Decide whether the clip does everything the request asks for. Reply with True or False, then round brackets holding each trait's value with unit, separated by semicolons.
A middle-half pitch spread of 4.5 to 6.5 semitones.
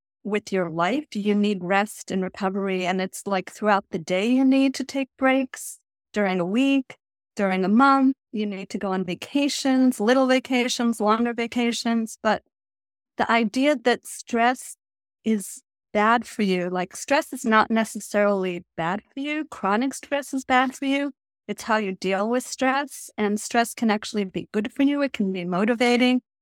True (4.8 semitones)